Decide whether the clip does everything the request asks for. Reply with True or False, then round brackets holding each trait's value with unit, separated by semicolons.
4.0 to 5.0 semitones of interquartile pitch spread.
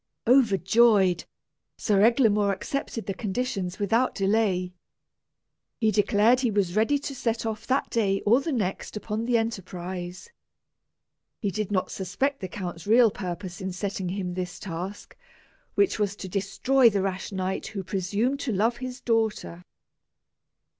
False (3.6 semitones)